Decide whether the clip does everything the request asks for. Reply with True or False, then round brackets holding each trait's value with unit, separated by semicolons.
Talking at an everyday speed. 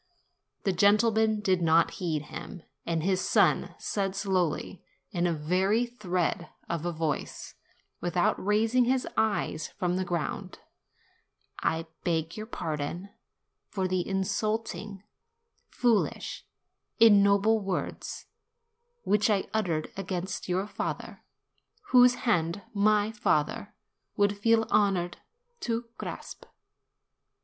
False (110 wpm)